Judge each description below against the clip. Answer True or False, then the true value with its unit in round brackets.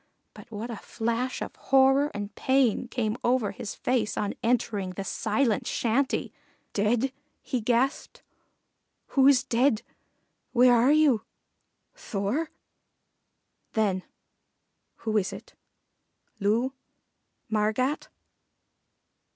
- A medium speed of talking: False (100 wpm)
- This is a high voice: True (235 Hz)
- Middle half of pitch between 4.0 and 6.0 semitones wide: False (3.5 semitones)